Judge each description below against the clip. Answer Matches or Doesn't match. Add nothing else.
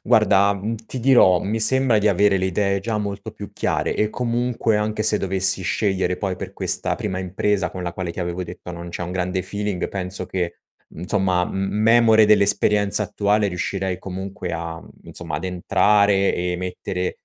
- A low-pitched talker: Matches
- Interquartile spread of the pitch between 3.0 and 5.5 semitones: Doesn't match